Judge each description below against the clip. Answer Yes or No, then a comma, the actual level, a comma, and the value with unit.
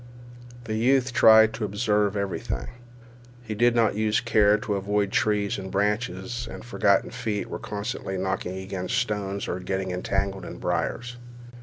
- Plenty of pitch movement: No, average, 2.7 semitones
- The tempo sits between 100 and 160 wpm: Yes, average, 155 wpm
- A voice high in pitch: No, low, 105 Hz